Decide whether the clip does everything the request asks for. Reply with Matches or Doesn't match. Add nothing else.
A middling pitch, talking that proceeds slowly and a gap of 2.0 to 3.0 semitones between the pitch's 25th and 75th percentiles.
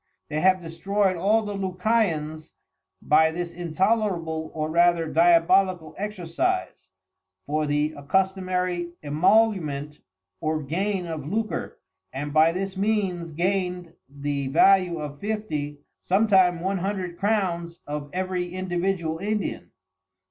Doesn't match